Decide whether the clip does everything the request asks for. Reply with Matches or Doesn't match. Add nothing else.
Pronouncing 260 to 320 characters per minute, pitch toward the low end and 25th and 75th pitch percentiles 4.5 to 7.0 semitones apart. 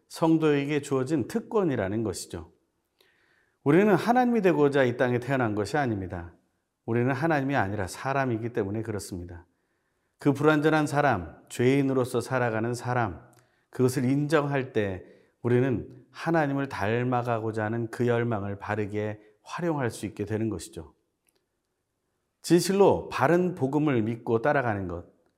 Matches